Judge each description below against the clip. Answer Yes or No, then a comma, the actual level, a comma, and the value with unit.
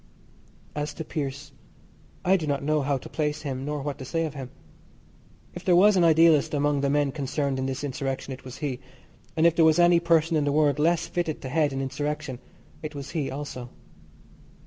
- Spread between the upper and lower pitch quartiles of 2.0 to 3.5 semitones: Yes, narrow, 2.6 semitones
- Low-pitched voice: No, medium, 145 Hz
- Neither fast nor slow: No, fast, 210 wpm